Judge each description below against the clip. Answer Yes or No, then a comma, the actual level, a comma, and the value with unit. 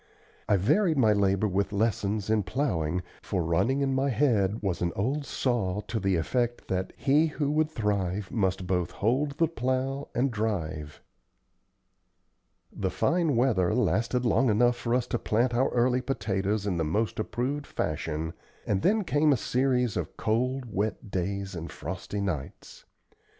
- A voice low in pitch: Yes, low, 110 Hz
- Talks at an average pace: Yes, average, 160 wpm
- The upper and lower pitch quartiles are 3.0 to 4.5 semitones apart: No, wide, 5.4 semitones